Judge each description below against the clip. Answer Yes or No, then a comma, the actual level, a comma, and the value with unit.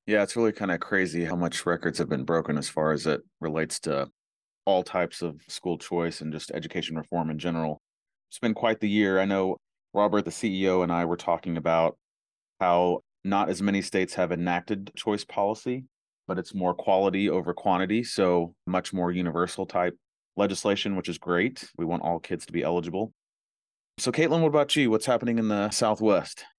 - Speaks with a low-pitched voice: Yes, very low, 90 Hz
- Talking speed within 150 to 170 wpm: No, average, 190 wpm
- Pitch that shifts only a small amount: No, average, 3.3 semitones